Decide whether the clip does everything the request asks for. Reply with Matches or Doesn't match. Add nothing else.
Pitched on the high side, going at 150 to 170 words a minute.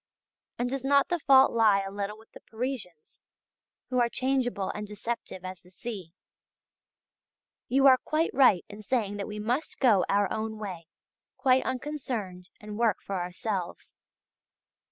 Matches